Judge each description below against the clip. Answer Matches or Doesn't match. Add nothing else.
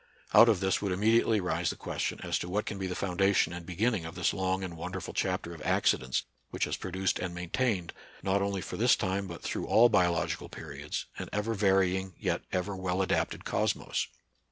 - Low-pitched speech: Matches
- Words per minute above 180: Matches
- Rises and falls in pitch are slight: Matches